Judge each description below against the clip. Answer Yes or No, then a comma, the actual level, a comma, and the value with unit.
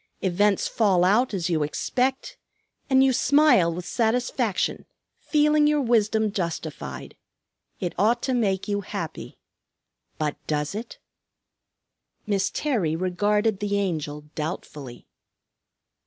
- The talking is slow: Yes, slow, 110 wpm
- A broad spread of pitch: Yes, wide, 5.9 semitones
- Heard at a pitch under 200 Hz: No, high, 205 Hz